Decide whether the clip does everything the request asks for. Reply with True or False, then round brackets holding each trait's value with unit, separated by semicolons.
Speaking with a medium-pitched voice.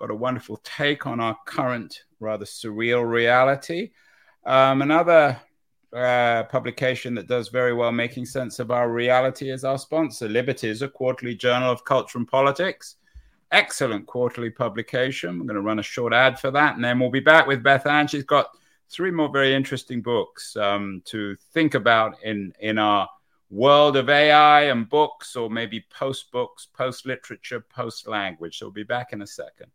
False (125 Hz)